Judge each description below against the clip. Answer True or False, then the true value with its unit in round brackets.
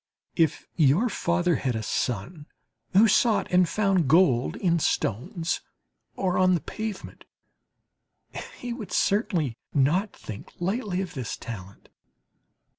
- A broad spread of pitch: True (6.3 semitones)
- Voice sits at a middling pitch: True (175 Hz)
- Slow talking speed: True (120 wpm)